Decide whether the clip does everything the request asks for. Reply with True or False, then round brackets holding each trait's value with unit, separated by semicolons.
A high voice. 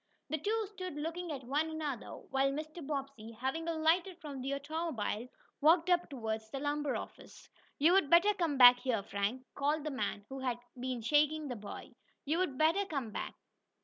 True (290 Hz)